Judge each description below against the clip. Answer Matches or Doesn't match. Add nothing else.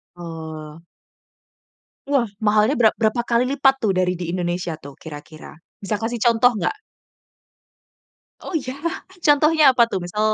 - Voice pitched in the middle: Doesn't match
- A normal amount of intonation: Doesn't match